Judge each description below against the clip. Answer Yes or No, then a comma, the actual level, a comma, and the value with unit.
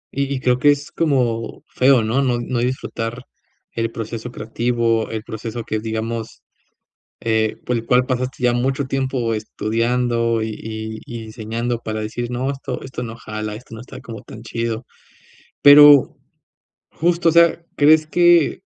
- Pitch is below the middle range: Yes, low, 120 Hz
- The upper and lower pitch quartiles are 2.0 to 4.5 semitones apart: Yes, average, 2.8 semitones